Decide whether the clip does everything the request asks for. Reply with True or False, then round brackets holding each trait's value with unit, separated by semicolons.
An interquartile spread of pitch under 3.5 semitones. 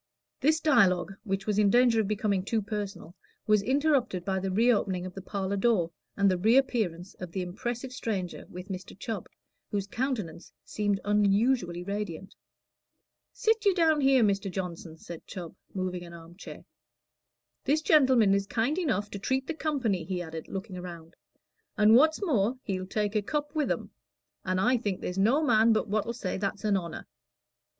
False (4.7 semitones)